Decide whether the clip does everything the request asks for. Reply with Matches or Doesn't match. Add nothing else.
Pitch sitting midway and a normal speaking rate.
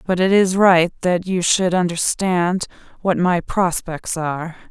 Matches